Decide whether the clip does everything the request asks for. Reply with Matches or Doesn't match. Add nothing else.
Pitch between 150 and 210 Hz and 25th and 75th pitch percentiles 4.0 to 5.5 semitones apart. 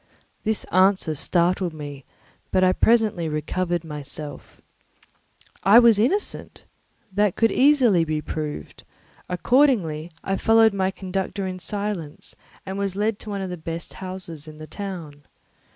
Matches